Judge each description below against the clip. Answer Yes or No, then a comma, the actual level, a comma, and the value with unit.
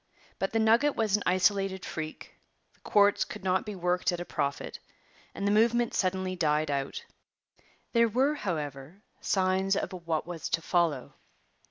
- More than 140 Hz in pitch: Yes, medium, 185 Hz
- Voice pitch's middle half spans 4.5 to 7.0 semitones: No, average, 3.7 semitones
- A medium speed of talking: Yes, average, 160 wpm